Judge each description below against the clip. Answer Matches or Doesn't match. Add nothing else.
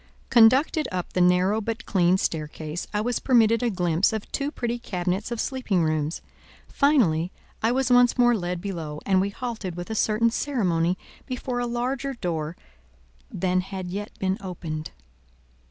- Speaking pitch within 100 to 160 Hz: Doesn't match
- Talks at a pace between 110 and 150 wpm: Doesn't match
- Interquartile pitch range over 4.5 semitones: Matches